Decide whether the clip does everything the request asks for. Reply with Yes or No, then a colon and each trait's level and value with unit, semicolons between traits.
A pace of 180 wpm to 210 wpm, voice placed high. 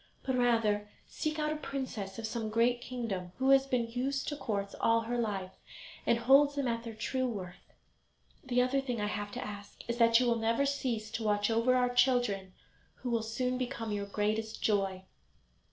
Yes: average, 195 wpm; high, 230 Hz